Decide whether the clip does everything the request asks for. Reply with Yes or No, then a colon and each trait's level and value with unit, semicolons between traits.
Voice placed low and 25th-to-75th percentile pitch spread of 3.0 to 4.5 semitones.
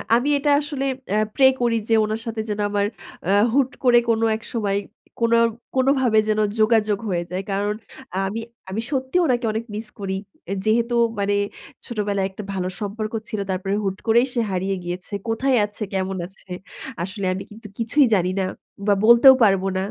No: high, 215 Hz; average, 3.3 semitones